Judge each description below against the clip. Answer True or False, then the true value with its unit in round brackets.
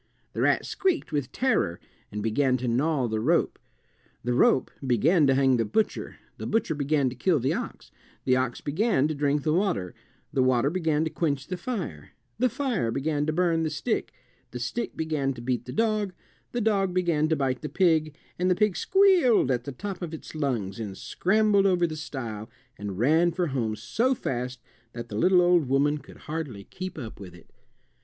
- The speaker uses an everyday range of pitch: False (6.3 semitones)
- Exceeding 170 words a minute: True (195 wpm)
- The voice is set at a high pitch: False (150 Hz)